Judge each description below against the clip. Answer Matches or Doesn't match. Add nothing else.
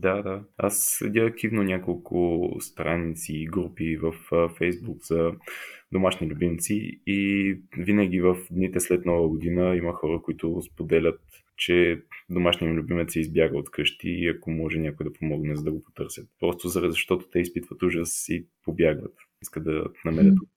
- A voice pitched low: Matches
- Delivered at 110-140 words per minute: Doesn't match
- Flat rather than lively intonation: Matches